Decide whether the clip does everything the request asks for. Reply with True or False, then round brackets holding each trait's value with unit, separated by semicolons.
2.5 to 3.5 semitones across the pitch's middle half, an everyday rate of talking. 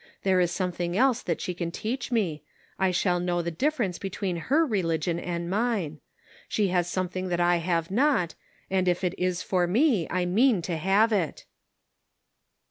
True (3.1 semitones; 175 wpm)